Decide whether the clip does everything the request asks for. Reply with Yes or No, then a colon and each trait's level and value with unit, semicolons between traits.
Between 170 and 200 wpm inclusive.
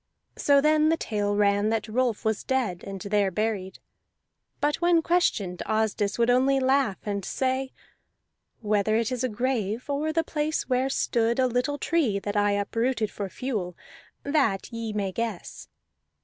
No: average, 160 wpm